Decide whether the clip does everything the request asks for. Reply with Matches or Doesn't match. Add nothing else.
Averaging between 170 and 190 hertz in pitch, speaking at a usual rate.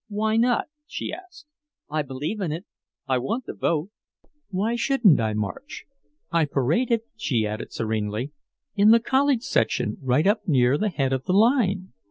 Matches